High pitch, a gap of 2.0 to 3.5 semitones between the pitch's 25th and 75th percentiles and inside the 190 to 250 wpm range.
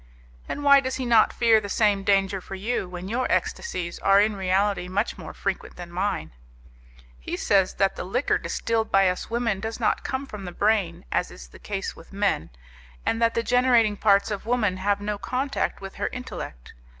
Yes: high, 205 Hz; average, 3.2 semitones; average, 200 wpm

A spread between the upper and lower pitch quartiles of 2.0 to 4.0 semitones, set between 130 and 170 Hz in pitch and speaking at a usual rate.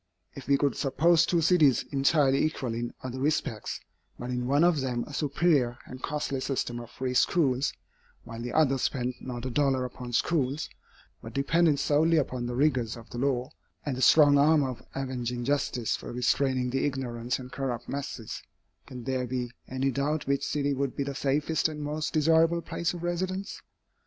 Yes: average, 3.1 semitones; low, 135 Hz; average, 180 wpm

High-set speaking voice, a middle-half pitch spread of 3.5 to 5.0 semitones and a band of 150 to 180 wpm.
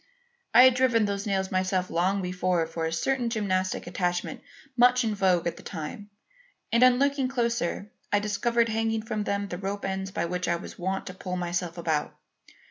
No: high, 195 Hz; average, 4.1 semitones; average, 190 wpm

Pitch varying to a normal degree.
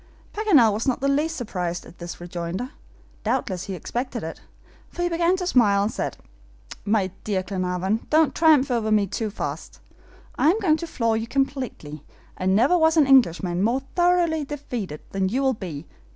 No: wide, 7.8 semitones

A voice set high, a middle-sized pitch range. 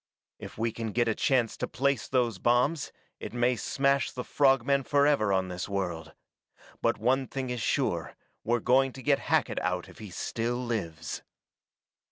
No: low, 120 Hz; average, 3.9 semitones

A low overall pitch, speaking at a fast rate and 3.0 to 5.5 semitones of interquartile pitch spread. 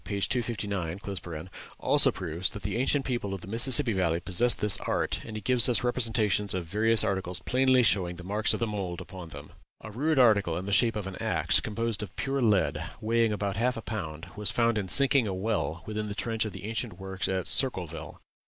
Yes: low, 105 Hz; fast, 210 wpm; average, 3.7 semitones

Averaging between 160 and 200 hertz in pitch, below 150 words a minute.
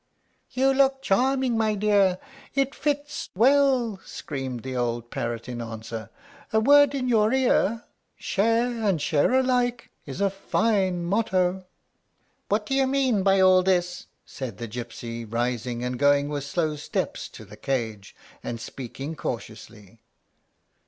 Yes: medium, 185 Hz; average, 140 wpm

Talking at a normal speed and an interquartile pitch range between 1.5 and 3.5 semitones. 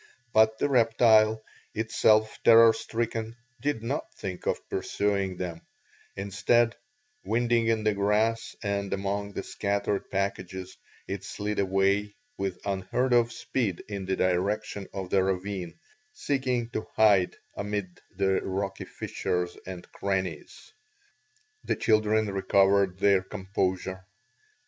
No: slow, 120 wpm; narrow, 2.5 semitones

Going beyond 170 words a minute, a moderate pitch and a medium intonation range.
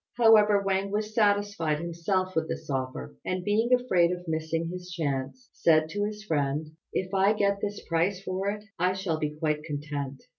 Yes: average, 180 wpm; medium, 180 Hz; average, 4.5 semitones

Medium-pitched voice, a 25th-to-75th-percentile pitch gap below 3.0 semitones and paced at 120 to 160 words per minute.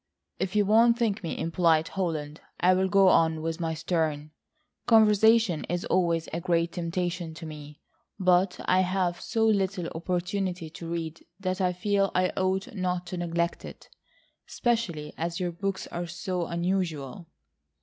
Yes: medium, 180 Hz; narrow, 2.5 semitones; average, 150 wpm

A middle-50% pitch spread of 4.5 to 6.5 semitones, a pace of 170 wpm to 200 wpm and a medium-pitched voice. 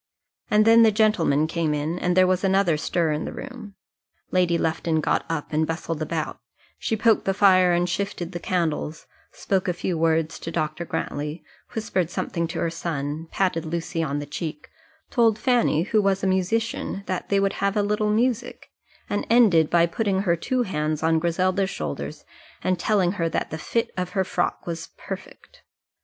No: average, 3.5 semitones; average, 185 wpm; medium, 180 Hz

